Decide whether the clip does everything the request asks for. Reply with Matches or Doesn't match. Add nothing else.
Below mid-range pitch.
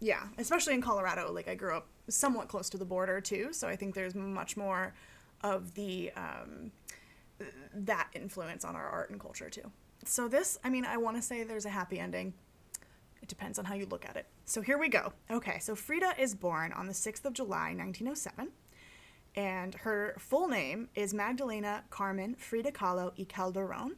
Doesn't match